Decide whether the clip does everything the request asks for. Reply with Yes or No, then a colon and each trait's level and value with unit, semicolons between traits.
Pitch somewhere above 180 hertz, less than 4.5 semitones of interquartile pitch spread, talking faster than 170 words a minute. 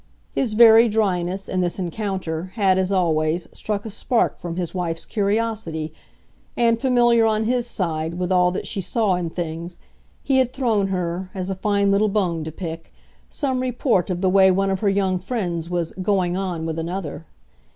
Yes: high, 190 Hz; average, 3.8 semitones; average, 185 wpm